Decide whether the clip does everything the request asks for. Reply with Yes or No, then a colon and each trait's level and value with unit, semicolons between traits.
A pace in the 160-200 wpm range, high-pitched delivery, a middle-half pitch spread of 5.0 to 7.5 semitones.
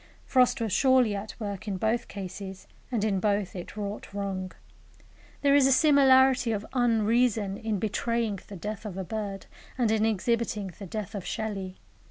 No: average, 170 wpm; high, 215 Hz; average, 2.9 semitones